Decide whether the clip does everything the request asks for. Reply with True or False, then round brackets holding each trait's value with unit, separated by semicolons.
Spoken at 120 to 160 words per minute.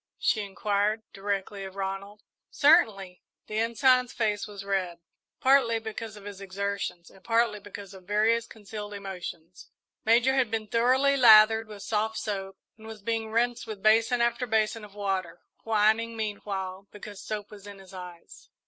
True (155 wpm)